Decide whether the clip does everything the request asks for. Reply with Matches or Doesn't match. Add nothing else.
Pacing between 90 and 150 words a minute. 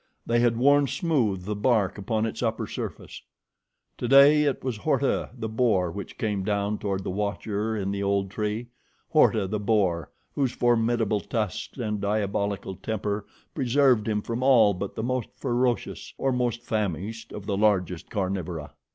Doesn't match